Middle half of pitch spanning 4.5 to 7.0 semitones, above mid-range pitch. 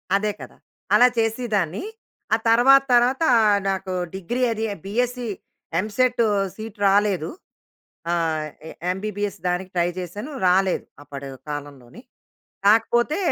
Yes: average, 5.0 semitones; high, 205 Hz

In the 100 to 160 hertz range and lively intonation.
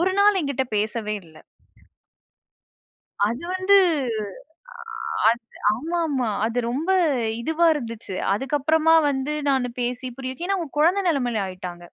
No: very high, 265 Hz; wide, 5.9 semitones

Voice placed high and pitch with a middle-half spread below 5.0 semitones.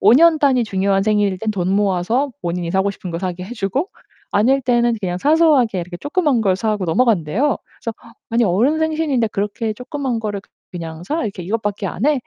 No: high, 215 Hz; wide, 5.4 semitones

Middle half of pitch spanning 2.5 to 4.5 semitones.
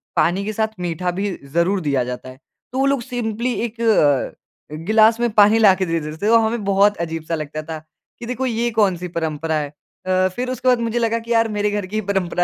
No: wide, 5.5 semitones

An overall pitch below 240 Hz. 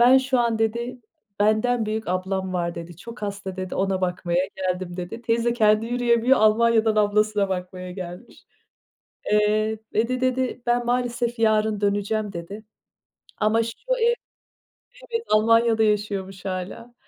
Yes: high, 215 Hz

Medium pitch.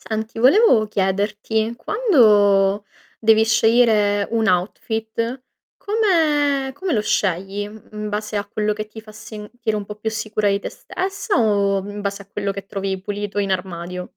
No: high, 215 Hz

